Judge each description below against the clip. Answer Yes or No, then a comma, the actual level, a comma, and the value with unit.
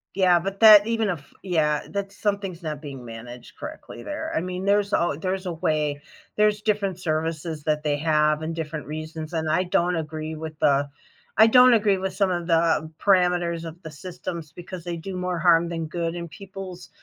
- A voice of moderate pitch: Yes, medium, 170 Hz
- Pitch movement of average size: Yes, average, 3.6 semitones